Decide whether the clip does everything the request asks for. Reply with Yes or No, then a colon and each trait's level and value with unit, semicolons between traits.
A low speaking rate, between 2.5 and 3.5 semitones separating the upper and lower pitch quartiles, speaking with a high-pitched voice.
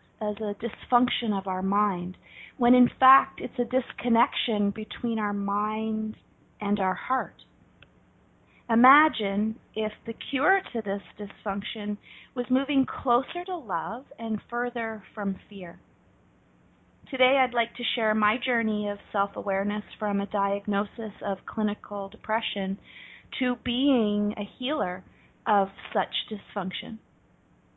Yes: slow, 125 wpm; average, 3.2 semitones; high, 215 Hz